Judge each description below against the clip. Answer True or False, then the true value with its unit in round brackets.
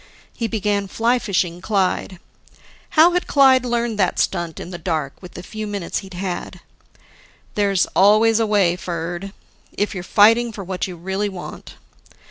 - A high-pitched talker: True (200 Hz)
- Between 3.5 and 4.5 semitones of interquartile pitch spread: True (3.8 semitones)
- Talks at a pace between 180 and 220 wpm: False (160 wpm)